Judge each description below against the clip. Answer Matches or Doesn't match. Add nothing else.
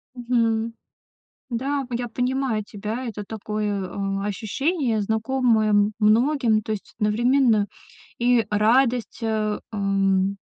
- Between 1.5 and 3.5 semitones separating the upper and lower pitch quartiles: Matches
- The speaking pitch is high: Matches